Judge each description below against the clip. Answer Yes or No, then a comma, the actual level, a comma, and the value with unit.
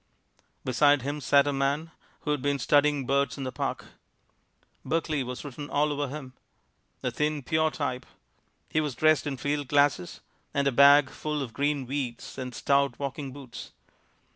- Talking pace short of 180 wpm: Yes, average, 165 wpm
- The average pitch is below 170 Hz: Yes, medium, 140 Hz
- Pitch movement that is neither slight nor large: No, narrow, 1.9 semitones